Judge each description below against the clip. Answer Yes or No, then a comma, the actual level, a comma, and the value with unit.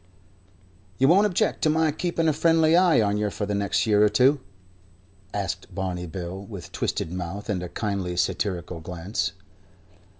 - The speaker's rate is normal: Yes, average, 165 wpm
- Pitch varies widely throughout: Yes, wide, 8.8 semitones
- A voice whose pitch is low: Yes, low, 105 Hz